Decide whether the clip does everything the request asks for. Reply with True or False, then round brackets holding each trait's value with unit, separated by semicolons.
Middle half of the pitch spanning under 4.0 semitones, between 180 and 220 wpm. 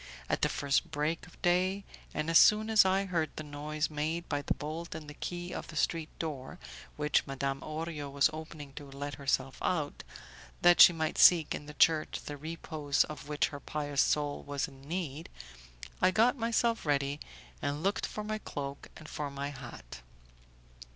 True (3.0 semitones; 185 wpm)